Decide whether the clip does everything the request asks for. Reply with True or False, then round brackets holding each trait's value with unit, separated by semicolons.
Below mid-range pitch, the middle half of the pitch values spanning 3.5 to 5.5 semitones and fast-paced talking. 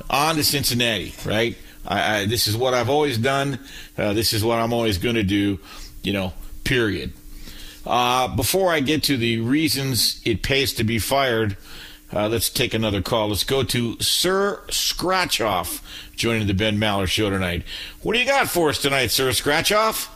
False (115 Hz; 4.7 semitones; 180 wpm)